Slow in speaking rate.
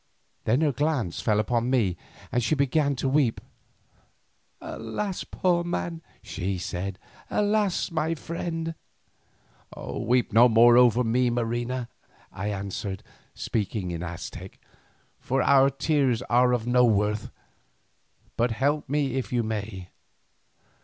Yes: slow, 120 wpm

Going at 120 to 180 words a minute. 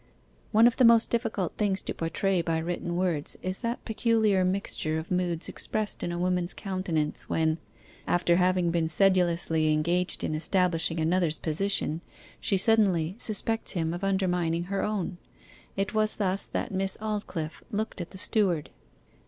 Yes: average, 155 wpm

